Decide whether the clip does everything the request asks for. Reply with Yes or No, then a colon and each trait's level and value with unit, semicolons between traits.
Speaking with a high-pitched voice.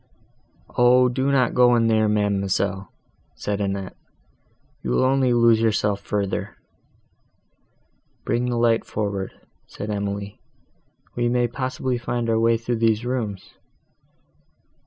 No: low, 115 Hz